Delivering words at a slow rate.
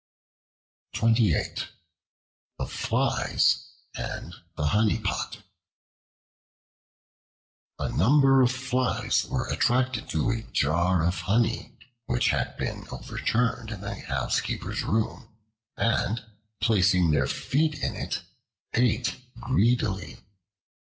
Yes: slow, 95 wpm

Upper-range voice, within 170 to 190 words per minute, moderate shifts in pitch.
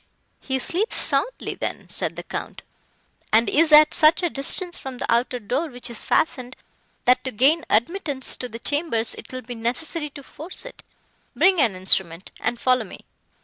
Yes: very high, 260 Hz; average, 180 wpm; average, 4.9 semitones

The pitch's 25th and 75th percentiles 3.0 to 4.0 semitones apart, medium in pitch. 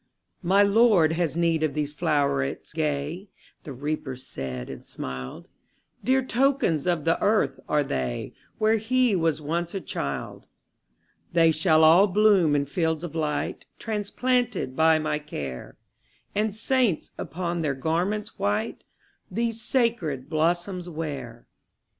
No: wide, 5.6 semitones; medium, 165 Hz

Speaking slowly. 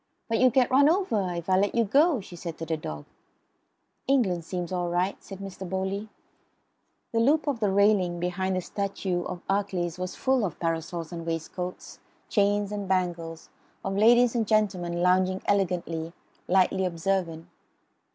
No: average, 160 wpm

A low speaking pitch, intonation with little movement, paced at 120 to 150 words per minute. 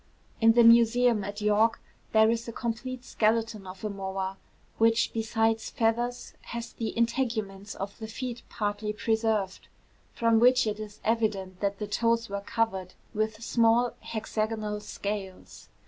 No: high, 220 Hz; narrow, 1.9 semitones; average, 145 wpm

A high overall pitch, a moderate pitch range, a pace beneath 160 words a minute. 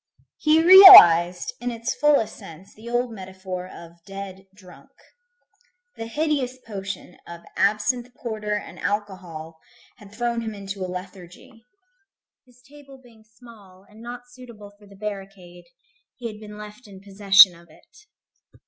Yes: high, 210 Hz; average, 4.2 semitones; average, 140 wpm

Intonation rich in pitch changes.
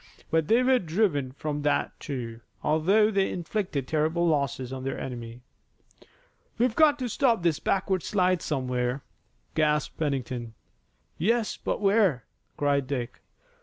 Yes: wide, 6.9 semitones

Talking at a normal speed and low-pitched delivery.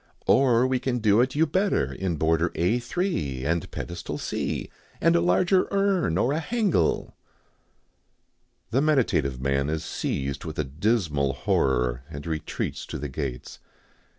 Yes: average, 150 wpm; very low, 90 Hz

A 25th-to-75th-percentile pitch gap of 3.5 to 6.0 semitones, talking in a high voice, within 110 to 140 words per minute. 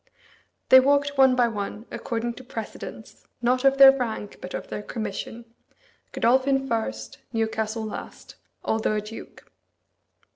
No: average, 3.1 semitones; high, 235 Hz; slow, 135 wpm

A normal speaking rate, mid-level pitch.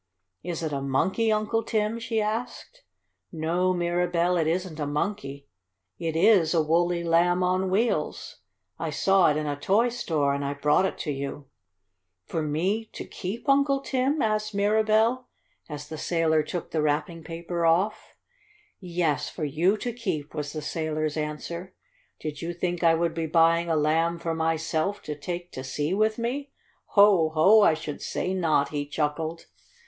Yes: average, 170 wpm; medium, 170 Hz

